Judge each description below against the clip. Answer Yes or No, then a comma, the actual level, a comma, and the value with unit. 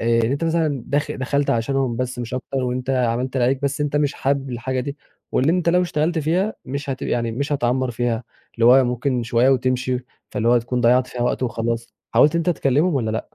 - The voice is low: Yes, low, 130 Hz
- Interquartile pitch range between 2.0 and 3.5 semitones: Yes, average, 2.7 semitones